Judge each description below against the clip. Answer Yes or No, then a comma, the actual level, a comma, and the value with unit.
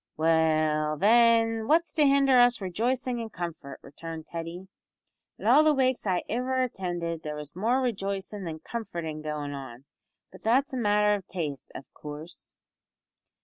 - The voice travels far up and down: Yes, wide, 7.2 semitones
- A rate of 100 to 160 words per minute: Yes, average, 150 wpm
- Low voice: No, high, 190 Hz